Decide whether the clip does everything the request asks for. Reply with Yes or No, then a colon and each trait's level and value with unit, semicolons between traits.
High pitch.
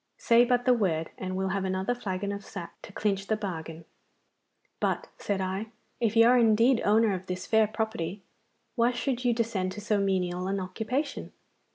Yes: high, 205 Hz